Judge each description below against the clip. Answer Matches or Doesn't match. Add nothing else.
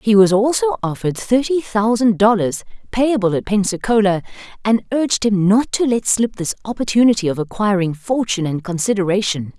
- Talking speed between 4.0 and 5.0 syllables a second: Doesn't match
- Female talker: Matches